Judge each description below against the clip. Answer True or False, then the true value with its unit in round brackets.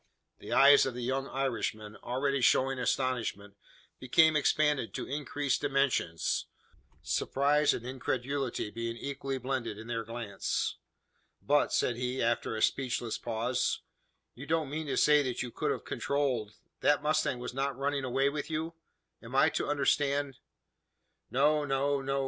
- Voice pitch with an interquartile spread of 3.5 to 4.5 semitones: False (2.8 semitones)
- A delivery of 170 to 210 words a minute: False (155 wpm)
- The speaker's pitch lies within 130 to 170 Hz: True (135 Hz)